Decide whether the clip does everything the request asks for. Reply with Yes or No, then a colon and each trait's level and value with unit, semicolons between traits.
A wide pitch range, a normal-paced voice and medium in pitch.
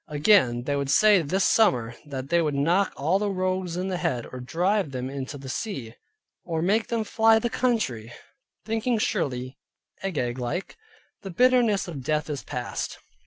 Yes: wide, 7.3 semitones; average, 170 wpm; medium, 170 Hz